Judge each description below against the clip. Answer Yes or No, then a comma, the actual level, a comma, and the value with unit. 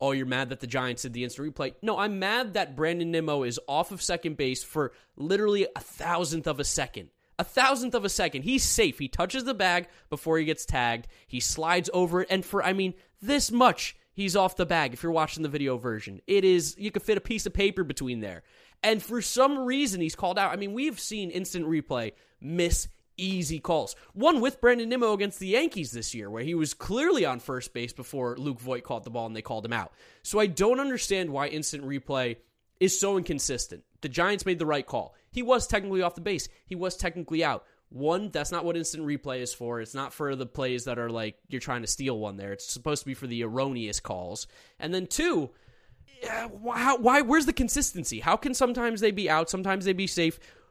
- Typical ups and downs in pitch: No, wide, 7.3 semitones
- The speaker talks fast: Yes, fast, 225 wpm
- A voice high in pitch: No, medium, 165 Hz